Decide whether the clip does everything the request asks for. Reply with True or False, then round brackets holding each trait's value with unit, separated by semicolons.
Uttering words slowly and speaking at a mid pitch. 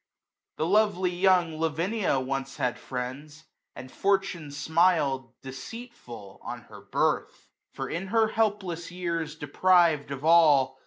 True (120 wpm; 165 Hz)